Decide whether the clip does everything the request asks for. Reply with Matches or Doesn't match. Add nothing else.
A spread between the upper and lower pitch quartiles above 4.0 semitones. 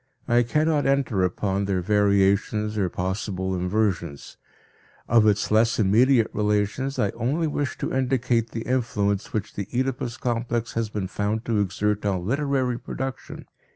Doesn't match